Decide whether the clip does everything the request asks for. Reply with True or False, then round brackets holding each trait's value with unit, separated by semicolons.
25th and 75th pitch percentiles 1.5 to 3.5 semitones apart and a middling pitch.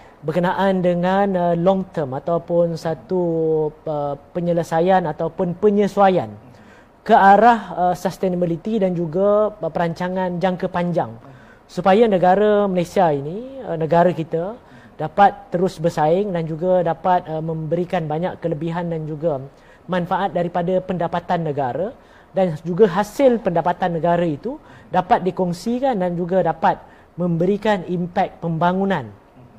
True (2.5 semitones; 175 Hz)